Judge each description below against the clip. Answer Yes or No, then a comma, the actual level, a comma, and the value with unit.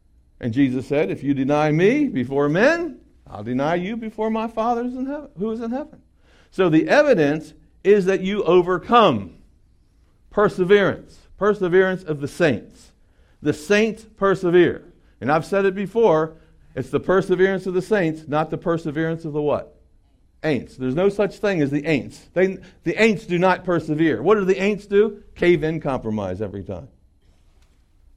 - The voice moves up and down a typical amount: No, wide, 7.0 semitones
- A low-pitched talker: No, medium, 170 Hz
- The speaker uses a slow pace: No, average, 165 wpm